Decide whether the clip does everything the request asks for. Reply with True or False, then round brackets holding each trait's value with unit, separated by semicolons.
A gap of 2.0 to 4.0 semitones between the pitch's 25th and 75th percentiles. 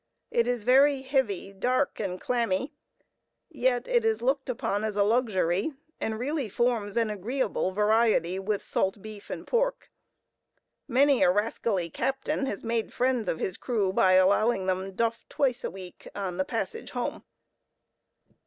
False (4.9 semitones)